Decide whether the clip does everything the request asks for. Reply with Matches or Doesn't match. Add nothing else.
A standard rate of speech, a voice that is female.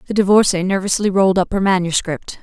Matches